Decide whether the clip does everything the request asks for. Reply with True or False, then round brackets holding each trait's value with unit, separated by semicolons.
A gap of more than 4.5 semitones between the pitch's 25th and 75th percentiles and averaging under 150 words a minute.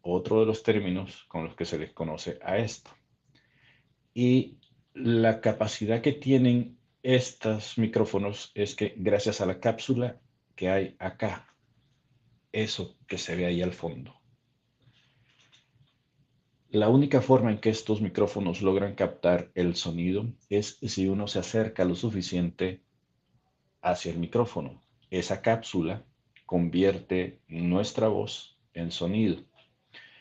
True (5.1 semitones; 125 wpm)